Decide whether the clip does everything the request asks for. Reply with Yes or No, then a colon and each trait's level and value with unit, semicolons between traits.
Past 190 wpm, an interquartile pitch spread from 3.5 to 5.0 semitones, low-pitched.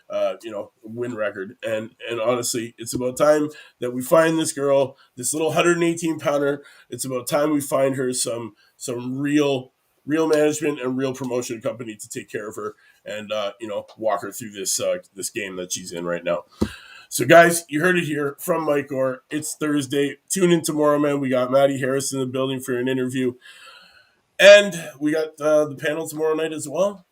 No: average, 200 wpm; average, 3.8 semitones; medium, 145 Hz